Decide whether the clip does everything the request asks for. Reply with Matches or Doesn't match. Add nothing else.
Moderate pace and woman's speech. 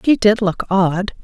Matches